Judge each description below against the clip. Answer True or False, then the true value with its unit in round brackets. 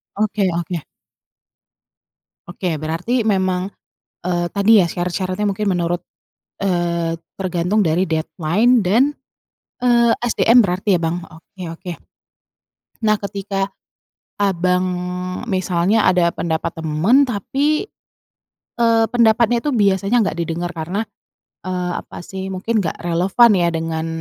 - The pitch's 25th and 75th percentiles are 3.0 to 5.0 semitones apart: True (3.7 semitones)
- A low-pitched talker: False (185 Hz)